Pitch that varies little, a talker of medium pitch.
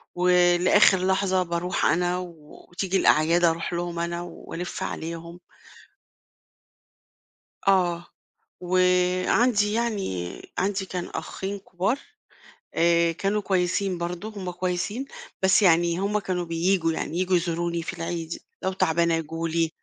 Yes: narrow, 2.0 semitones; medium, 180 Hz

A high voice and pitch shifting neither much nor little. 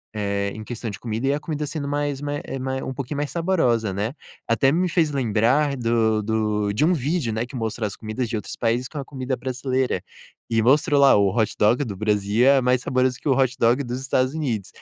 No: low, 125 Hz; average, 4.1 semitones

